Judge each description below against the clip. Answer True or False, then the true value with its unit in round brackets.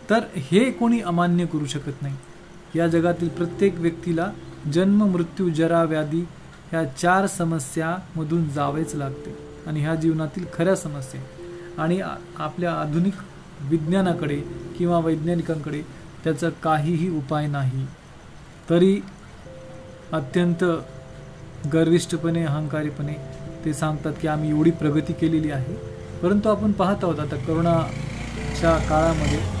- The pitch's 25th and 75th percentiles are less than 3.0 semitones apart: True (2.5 semitones)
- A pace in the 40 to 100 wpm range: False (110 wpm)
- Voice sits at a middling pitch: True (165 Hz)